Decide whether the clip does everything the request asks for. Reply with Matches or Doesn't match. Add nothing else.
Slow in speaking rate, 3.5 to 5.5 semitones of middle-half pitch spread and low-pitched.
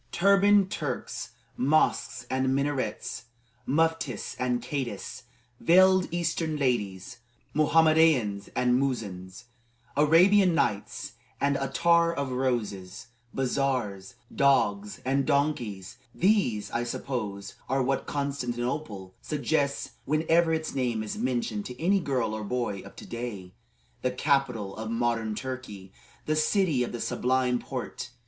Matches